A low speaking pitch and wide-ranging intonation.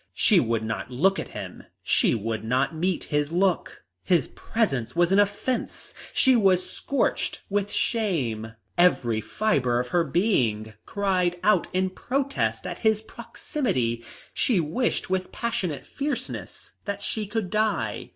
No: medium, 185 Hz; wide, 8.9 semitones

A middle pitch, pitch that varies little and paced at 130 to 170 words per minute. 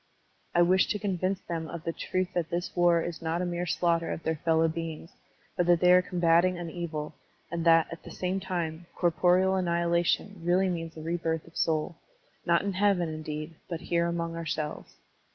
No: medium, 170 Hz; narrow, 1.5 semitones; average, 190 wpm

